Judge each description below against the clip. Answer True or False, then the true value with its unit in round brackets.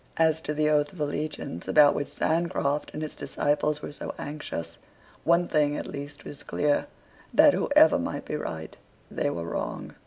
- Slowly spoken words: False (175 wpm)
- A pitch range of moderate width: False (1.1 semitones)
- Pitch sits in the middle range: True (150 Hz)